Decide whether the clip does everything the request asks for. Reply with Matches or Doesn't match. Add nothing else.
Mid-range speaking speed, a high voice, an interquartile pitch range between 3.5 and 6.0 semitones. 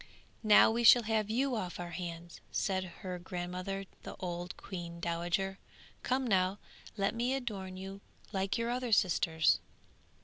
Matches